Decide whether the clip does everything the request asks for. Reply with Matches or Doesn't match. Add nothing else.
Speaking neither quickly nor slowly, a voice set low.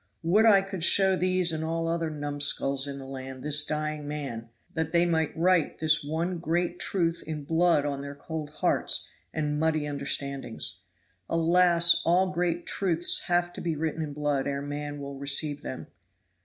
Doesn't match